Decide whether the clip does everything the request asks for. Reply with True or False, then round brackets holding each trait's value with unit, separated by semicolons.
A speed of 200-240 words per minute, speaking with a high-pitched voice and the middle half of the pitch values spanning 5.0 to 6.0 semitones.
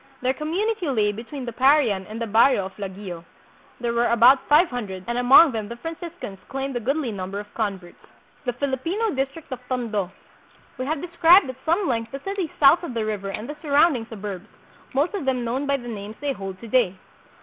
True (205 wpm; 245 Hz; 5.5 semitones)